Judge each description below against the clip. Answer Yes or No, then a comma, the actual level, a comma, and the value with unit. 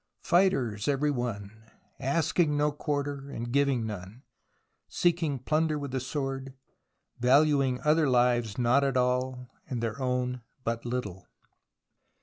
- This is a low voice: Yes, low, 130 Hz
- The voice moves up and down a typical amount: Yes, average, 3.0 semitones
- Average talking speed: No, slow, 120 wpm